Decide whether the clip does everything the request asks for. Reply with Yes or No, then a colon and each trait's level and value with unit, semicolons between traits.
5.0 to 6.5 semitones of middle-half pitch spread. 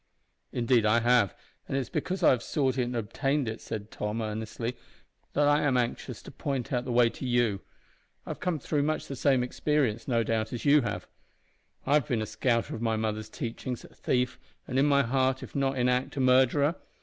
No: average, 3.0 semitones